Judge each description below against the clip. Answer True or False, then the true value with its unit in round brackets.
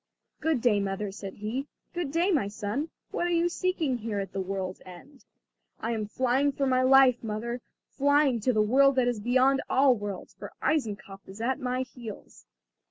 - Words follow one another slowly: False (185 wpm)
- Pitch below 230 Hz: False (245 Hz)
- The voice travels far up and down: False (4.7 semitones)